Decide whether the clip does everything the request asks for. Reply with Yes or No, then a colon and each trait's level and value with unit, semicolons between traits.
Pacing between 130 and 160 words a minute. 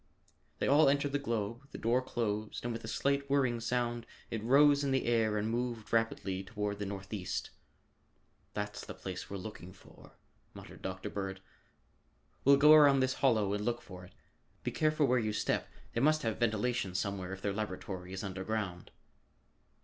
No: average, 175 wpm